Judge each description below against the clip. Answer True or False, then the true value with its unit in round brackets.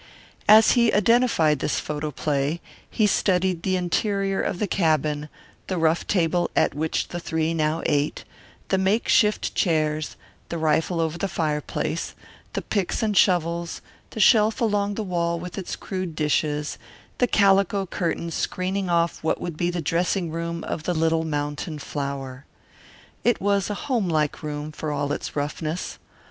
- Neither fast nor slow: True (155 wpm)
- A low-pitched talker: False (170 Hz)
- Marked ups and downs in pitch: False (4.0 semitones)